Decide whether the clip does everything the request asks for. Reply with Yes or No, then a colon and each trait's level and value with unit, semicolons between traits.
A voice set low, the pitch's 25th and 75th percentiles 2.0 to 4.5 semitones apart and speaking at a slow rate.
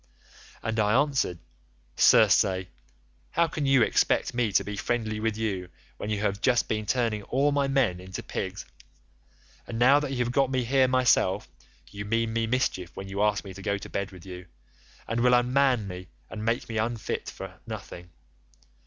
No: low, 115 Hz; average, 4.2 semitones; average, 185 wpm